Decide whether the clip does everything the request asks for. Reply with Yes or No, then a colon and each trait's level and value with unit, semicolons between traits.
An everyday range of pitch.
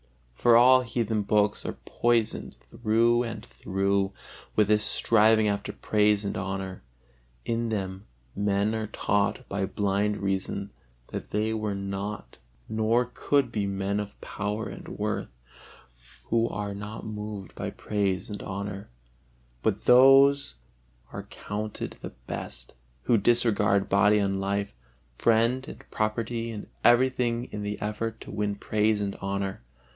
No: narrow, 2.3 semitones